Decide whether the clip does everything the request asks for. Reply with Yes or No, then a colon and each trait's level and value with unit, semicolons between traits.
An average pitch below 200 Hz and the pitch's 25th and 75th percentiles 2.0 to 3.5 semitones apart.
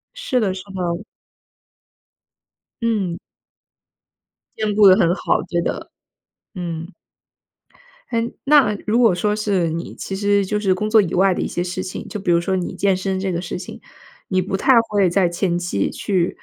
Yes: high, 190 Hz; average, 2.9 semitones